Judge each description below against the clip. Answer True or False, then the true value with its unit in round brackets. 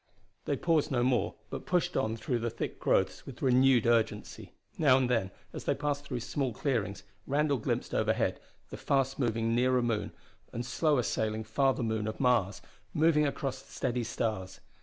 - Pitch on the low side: True (125 Hz)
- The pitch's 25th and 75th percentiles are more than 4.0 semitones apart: False (3.5 semitones)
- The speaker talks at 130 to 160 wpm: False (175 wpm)